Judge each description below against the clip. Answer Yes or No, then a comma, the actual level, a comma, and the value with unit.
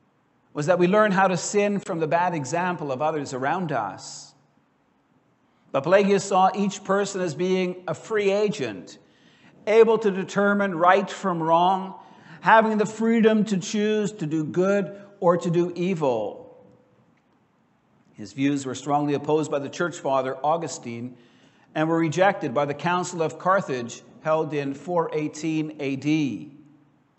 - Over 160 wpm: No, average, 145 wpm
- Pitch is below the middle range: No, medium, 175 Hz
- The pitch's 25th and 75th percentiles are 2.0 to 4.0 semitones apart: No, average, 4.6 semitones